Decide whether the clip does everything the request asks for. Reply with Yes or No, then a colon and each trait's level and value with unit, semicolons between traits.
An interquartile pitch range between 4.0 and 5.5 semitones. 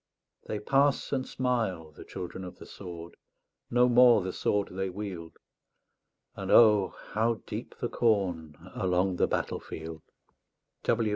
Yes: average, 4.8 semitones